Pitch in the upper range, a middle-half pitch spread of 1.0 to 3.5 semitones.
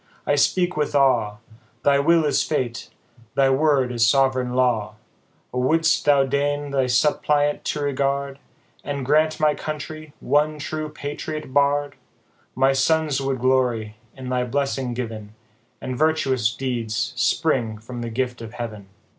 No: low, 135 Hz; average, 2.9 semitones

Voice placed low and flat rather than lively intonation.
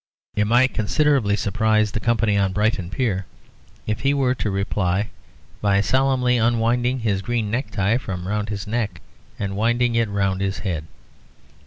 No: low, 110 Hz; average, 3.3 semitones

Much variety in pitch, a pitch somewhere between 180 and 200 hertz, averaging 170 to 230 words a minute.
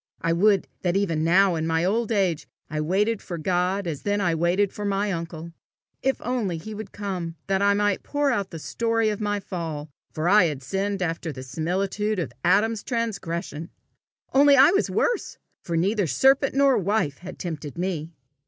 No: average, 4.0 semitones; high, 190 Hz; average, 185 wpm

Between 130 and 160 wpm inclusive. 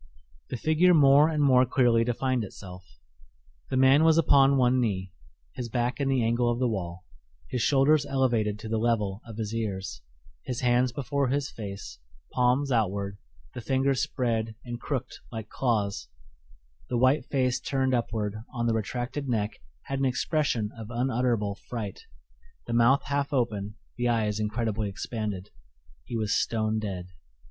Yes: average, 155 wpm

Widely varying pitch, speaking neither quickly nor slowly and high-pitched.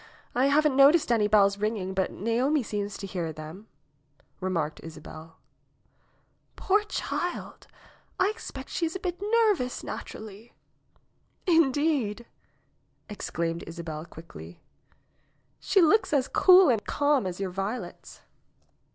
No: wide, 8.5 semitones; slow, 115 wpm; high, 220 Hz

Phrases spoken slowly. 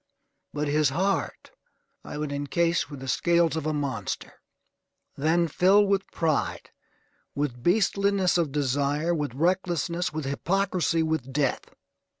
Yes: slow, 130 wpm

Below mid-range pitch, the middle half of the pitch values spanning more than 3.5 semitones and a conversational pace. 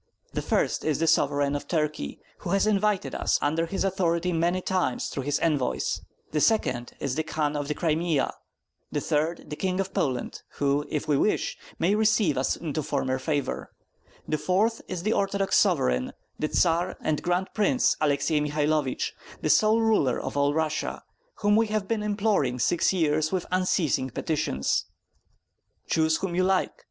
No: medium, 160 Hz; average, 4.7 semitones; average, 170 wpm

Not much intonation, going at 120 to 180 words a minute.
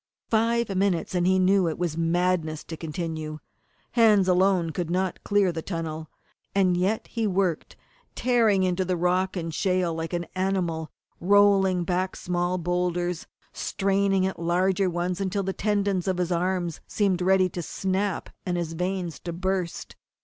Yes: narrow, 1.9 semitones; average, 160 wpm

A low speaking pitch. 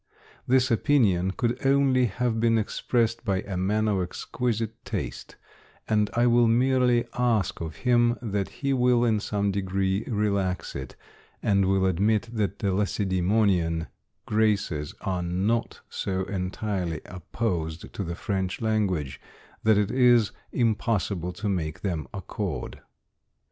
Yes: low, 105 Hz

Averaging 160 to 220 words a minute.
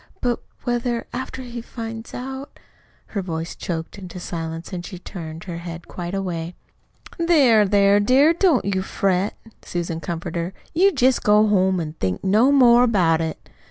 Yes: average, 165 wpm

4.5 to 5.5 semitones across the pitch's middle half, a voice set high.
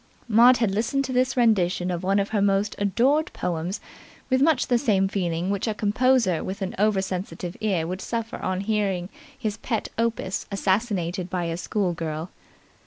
No: average, 3.9 semitones; high, 200 Hz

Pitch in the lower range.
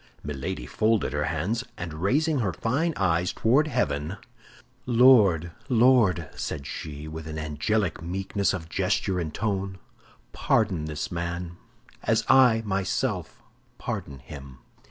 Yes: very low, 90 Hz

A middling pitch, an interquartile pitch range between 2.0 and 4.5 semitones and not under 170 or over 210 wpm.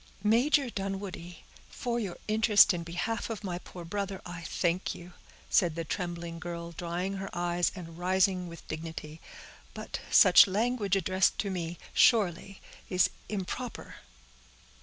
No: medium, 180 Hz; average, 2.8 semitones; average, 140 wpm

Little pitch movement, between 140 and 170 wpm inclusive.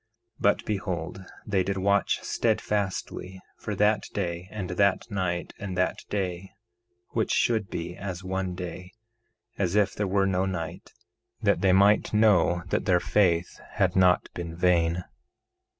Yes: narrow, 2.1 semitones; average, 150 wpm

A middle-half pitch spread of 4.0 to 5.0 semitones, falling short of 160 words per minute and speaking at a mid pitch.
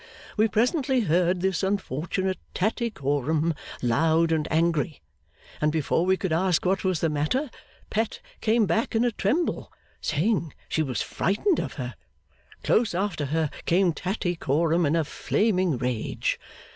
Yes: average, 4.7 semitones; average, 140 wpm; medium, 175 Hz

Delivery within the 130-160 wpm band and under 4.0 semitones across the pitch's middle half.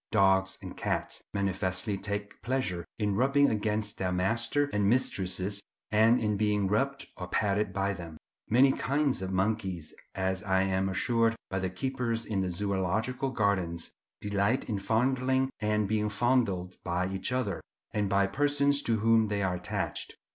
Yes: average, 155 wpm; average, 3.5 semitones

